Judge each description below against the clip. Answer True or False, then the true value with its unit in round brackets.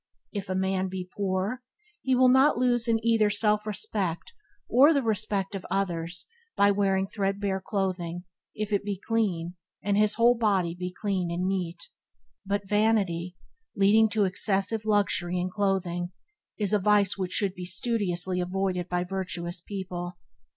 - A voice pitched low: False (195 Hz)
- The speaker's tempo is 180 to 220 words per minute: False (155 wpm)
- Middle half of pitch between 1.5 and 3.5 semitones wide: True (2.6 semitones)